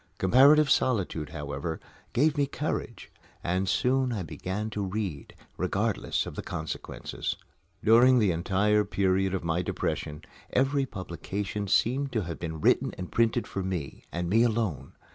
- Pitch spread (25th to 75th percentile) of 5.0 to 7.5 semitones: Yes, wide, 5.4 semitones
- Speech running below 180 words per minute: Yes, average, 145 wpm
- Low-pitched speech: Yes, low, 100 Hz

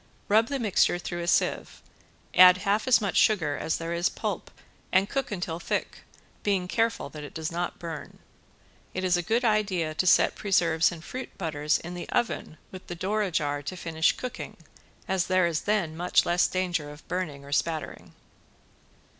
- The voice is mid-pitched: Yes, medium, 175 Hz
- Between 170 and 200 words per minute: Yes, average, 180 wpm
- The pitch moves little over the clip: No, average, 3.5 semitones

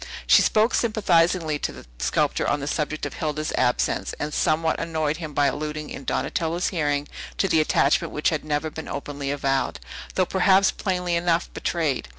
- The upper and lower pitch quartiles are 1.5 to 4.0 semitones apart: Yes, average, 2.8 semitones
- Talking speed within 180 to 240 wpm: No, average, 170 wpm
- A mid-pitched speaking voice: Yes, medium, 155 Hz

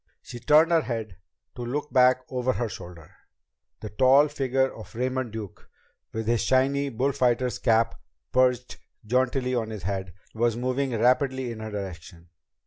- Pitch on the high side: No, low, 125 Hz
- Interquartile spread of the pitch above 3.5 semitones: No, average, 2.9 semitones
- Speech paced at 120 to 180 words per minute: Yes, average, 150 wpm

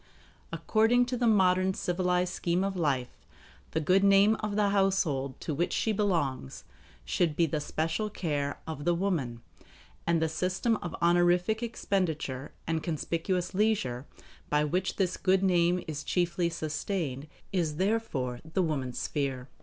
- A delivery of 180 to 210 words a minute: No, average, 145 wpm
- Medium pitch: Yes, medium, 175 Hz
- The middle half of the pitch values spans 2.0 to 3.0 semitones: No, average, 4.3 semitones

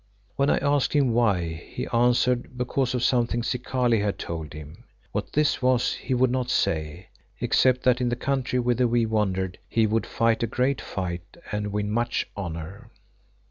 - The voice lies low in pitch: Yes, low, 120 Hz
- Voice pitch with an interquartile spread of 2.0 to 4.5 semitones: Yes, average, 3.9 semitones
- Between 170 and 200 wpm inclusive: Yes, average, 175 wpm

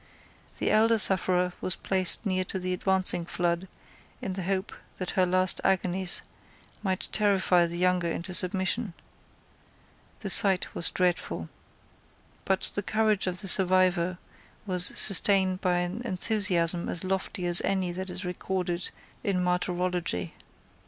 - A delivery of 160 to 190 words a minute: No, slow, 135 wpm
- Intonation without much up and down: Yes, narrow, 1.3 semitones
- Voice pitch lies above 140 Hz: Yes, medium, 185 Hz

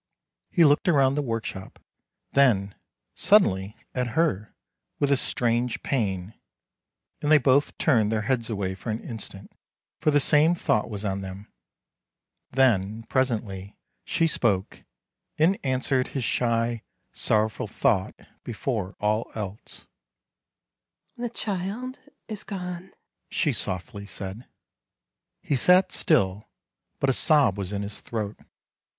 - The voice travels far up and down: Yes, wide, 6.2 semitones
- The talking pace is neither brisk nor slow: No, slow, 130 wpm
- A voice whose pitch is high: No, low, 115 Hz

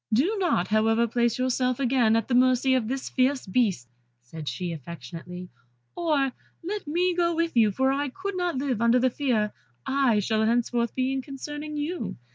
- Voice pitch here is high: Yes, very high, 255 Hz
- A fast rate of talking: No, average, 180 wpm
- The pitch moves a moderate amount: Yes, average, 4.7 semitones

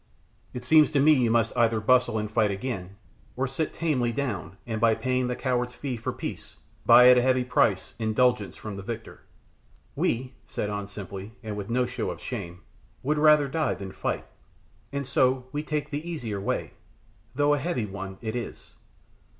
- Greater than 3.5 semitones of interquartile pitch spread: Yes, average, 4.0 semitones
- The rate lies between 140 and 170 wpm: No, average, 180 wpm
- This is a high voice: No, low, 125 Hz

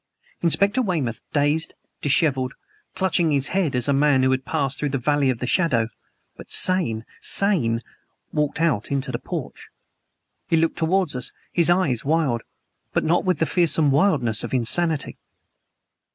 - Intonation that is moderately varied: Yes, average, 4.5 semitones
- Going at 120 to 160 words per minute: Yes, average, 155 wpm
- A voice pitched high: No, medium, 145 Hz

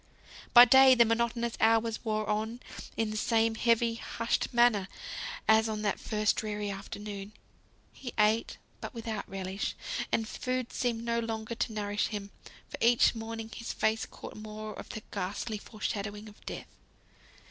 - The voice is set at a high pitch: Yes, high, 220 Hz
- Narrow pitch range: Yes, narrow, 1.6 semitones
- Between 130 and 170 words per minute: Yes, average, 160 wpm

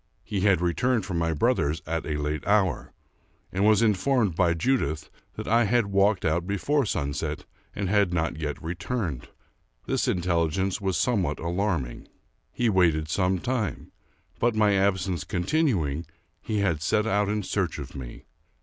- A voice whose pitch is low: Yes, very low, 95 Hz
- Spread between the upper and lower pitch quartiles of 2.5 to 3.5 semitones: No, average, 4.4 semitones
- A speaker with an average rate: Yes, average, 160 wpm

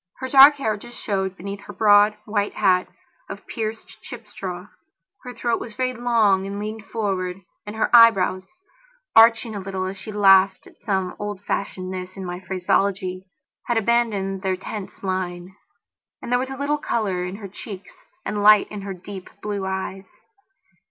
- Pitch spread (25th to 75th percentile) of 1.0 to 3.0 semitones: Yes, average, 2.7 semitones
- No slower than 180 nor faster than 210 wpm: No, average, 170 wpm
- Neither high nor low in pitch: No, high, 200 Hz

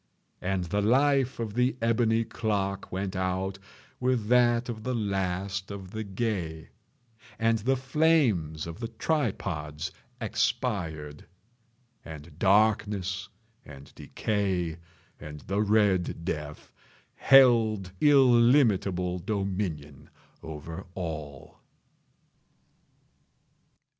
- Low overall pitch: Yes, low, 100 Hz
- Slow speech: Yes, slow, 95 wpm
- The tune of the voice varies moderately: Yes, average, 4.7 semitones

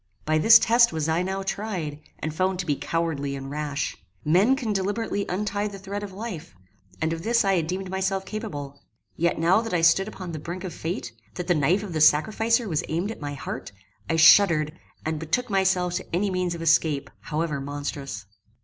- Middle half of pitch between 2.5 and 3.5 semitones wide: No, average, 4.2 semitones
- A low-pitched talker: No, medium, 175 Hz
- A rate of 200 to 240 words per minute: Yes, fast, 205 wpm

